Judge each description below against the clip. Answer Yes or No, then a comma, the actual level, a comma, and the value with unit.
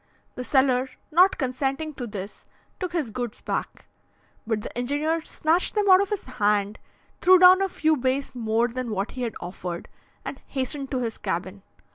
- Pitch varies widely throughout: Yes, wide, 6.0 semitones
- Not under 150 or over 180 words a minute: Yes, average, 175 wpm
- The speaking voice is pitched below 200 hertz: No, very high, 255 Hz